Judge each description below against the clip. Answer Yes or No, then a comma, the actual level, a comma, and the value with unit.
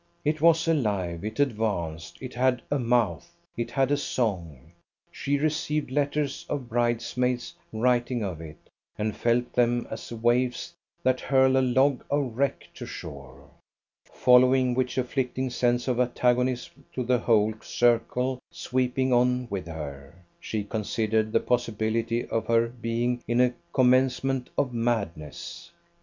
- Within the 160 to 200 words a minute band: No, average, 140 wpm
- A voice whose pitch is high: No, low, 120 Hz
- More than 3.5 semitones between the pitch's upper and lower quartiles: No, average, 2.8 semitones